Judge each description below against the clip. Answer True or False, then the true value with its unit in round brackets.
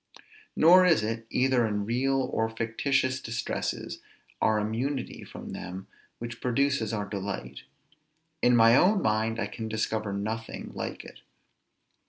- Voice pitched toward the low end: True (115 Hz)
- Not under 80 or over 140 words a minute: True (135 wpm)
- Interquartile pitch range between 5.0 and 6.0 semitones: False (3.2 semitones)